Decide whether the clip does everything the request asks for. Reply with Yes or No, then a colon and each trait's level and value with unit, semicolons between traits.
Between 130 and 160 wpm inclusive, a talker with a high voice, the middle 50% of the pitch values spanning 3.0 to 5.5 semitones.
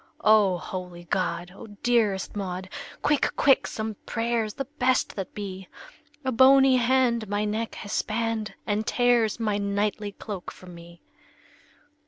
Yes: average, 140 wpm; high, 215 Hz; average, 3.6 semitones